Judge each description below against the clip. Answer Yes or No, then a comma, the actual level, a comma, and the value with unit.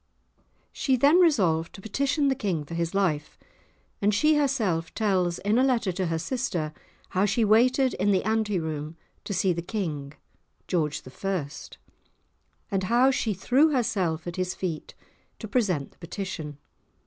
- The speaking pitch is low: No, high, 195 Hz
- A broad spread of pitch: Yes, wide, 6.1 semitones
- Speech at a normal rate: Yes, average, 160 wpm